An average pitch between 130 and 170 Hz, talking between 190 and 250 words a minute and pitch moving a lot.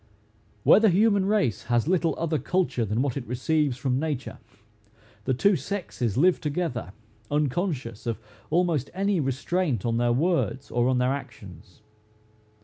No: medium, 140 Hz; average, 145 wpm; wide, 6.4 semitones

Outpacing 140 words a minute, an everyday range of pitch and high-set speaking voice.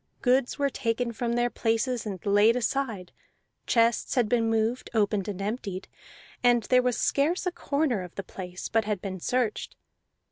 Yes: average, 170 wpm; average, 3.3 semitones; high, 230 Hz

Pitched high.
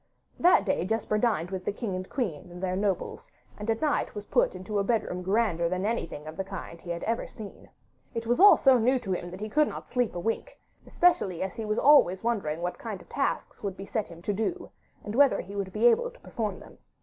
Yes: high, 205 Hz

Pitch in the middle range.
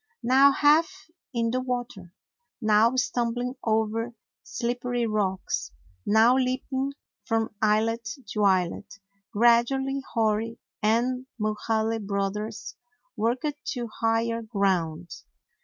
No: high, 230 Hz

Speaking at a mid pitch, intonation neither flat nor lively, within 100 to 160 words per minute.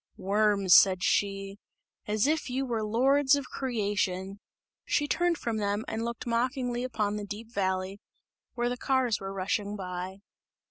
No: high, 210 Hz; average, 4.0 semitones; average, 150 wpm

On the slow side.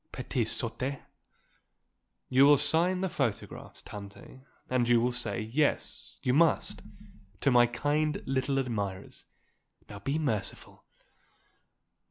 Yes: slow, 115 wpm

